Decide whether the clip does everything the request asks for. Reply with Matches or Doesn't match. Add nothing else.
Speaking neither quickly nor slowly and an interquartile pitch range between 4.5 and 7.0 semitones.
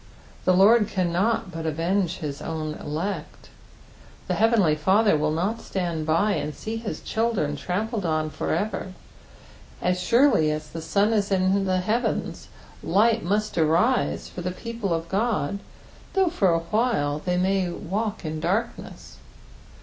Matches